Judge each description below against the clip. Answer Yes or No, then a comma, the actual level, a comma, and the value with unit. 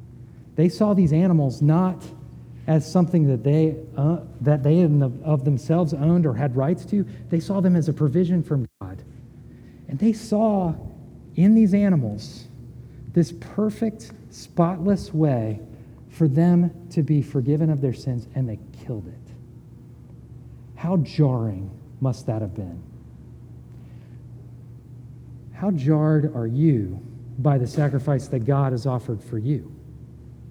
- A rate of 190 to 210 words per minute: No, slow, 135 wpm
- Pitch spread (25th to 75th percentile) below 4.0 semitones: No, wide, 5.5 semitones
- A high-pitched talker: No, medium, 145 Hz